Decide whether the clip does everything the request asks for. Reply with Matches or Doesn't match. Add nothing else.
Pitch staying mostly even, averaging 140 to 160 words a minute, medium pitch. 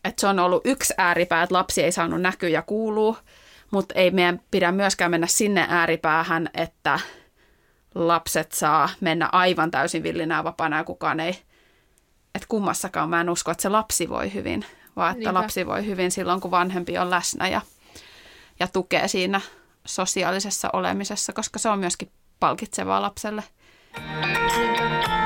Doesn't match